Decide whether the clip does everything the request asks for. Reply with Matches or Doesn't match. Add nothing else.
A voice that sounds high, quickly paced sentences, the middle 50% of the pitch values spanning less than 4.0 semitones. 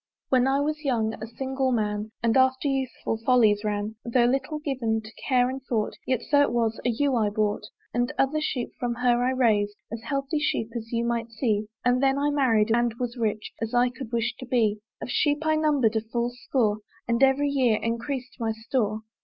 Matches